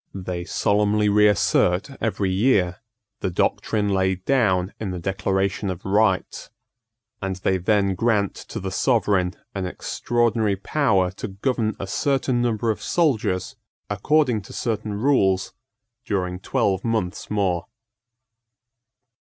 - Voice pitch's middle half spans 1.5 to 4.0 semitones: Yes, average, 2.9 semitones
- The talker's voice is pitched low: Yes, low, 100 Hz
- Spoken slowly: Yes, slow, 120 wpm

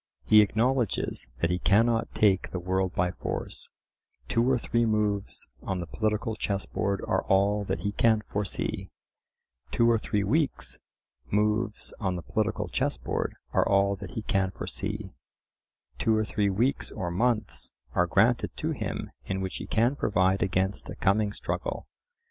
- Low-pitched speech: Yes, low, 100 Hz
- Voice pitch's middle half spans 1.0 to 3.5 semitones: Yes, average, 2.8 semitones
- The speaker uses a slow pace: No, average, 155 wpm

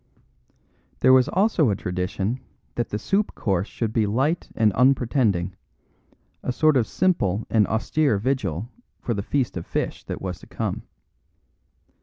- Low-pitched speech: Yes, low, 115 Hz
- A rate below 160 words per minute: Yes, average, 150 wpm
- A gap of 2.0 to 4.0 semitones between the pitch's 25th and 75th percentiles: No, average, 5.3 semitones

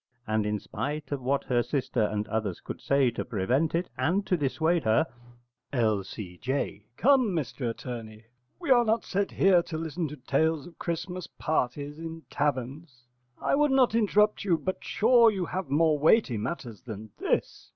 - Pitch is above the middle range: No, medium, 150 Hz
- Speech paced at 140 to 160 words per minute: No, average, 170 wpm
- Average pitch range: No, wide, 6.9 semitones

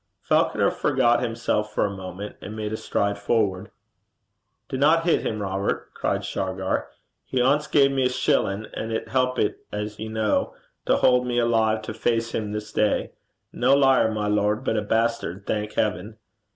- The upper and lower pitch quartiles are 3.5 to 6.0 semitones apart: No, average, 3.0 semitones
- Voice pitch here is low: Yes, low, 110 Hz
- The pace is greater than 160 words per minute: Yes, average, 170 wpm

